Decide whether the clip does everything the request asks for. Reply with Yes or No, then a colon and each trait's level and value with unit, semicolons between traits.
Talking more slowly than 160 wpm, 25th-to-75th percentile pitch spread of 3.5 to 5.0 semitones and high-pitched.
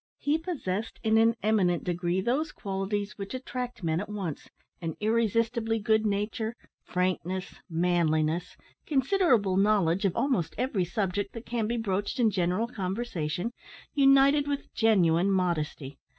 Yes: slow, 135 wpm; average, 4.5 semitones; high, 205 Hz